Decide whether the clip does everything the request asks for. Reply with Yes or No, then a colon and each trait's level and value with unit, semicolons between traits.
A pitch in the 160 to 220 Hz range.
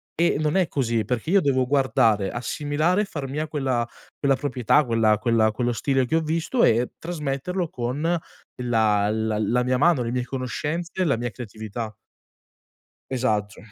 No: low, 130 Hz